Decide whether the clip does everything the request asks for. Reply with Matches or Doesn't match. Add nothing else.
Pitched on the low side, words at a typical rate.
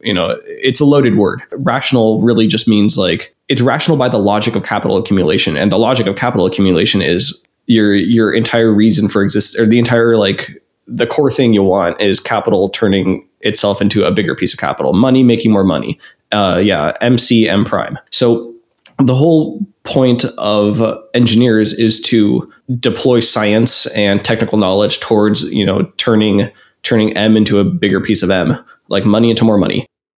Matches